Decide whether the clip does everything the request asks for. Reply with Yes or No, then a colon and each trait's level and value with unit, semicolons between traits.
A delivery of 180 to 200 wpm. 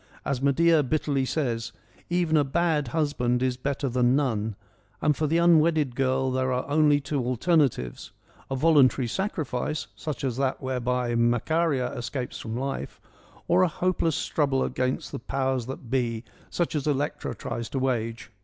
No: average, 165 wpm